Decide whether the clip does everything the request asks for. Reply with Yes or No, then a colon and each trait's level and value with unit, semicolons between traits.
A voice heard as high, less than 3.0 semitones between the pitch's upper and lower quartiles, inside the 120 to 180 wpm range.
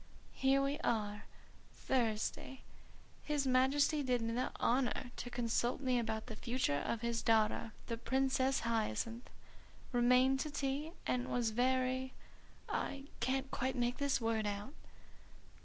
Yes: very high, 250 Hz; narrow, 2.6 semitones; average, 140 wpm